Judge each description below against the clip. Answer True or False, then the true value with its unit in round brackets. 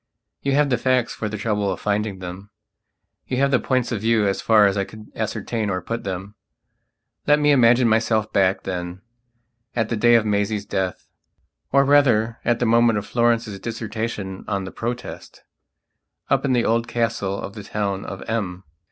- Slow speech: False (180 wpm)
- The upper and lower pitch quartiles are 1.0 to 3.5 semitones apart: True (3.0 semitones)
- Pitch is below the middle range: True (110 Hz)